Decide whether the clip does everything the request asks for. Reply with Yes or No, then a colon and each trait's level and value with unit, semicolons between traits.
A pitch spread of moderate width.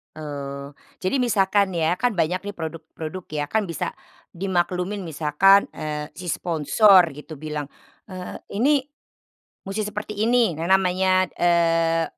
Yes: average, 3.8 semitones